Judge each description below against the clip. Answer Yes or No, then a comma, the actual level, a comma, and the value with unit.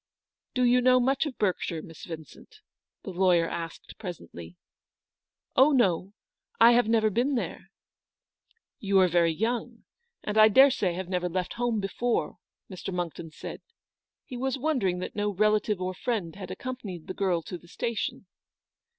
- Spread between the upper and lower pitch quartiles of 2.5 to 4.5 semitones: No, average, 5.3 semitones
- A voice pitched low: No, high, 200 Hz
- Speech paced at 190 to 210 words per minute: No, average, 175 wpm